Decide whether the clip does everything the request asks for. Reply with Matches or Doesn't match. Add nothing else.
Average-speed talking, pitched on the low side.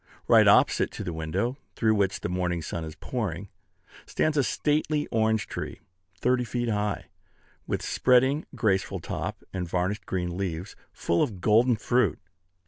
Matches